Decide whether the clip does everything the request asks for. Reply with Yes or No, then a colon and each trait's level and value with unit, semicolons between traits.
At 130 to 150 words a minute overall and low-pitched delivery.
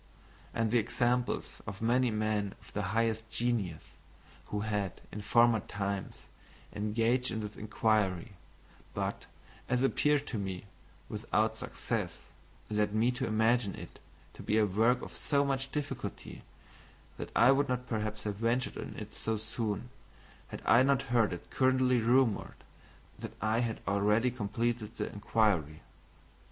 Yes: average, 145 wpm; low, 110 Hz